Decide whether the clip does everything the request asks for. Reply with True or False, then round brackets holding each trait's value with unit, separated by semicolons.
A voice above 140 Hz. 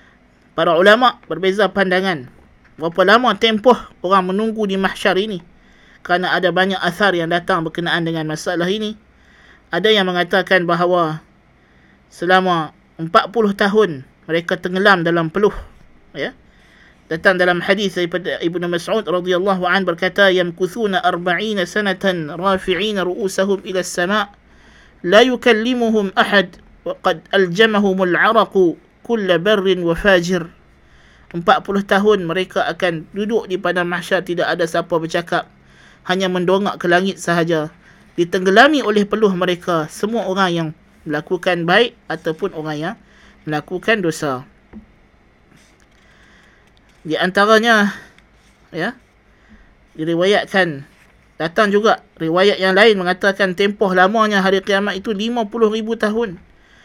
True (185 Hz)